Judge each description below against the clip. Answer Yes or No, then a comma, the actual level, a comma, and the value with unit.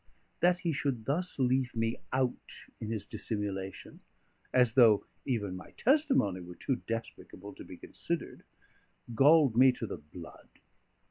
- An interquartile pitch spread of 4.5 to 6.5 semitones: Yes, average, 4.9 semitones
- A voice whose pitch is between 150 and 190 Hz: No, low, 120 Hz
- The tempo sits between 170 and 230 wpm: No, average, 140 wpm